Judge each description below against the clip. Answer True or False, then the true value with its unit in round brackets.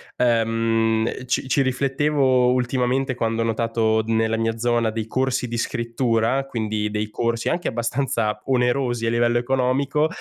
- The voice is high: False (120 Hz)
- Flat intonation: True (2.3 semitones)